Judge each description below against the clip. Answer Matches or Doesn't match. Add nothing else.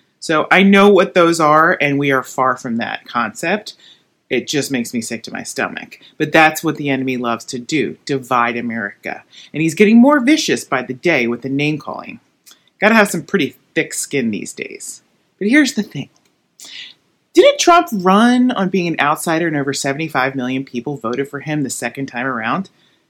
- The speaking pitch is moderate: Matches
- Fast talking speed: Doesn't match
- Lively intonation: Matches